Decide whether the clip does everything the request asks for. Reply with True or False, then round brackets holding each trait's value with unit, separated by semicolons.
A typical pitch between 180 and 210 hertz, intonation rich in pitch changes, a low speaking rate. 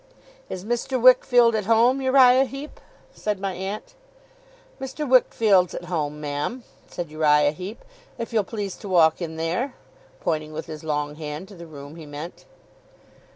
False (185 Hz; 7.4 semitones; 155 wpm)